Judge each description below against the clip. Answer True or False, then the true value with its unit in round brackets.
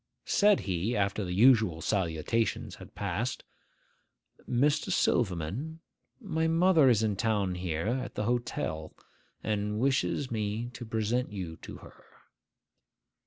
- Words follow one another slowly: True (120 wpm)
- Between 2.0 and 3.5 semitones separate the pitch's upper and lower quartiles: False (4.7 semitones)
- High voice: False (110 Hz)